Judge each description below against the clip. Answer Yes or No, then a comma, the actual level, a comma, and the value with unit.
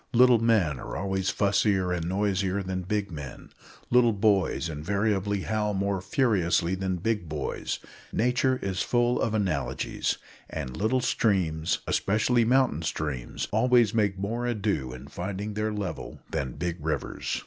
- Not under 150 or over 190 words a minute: No, average, 140 wpm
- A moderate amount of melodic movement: Yes, average, 3.9 semitones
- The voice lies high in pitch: No, low, 100 Hz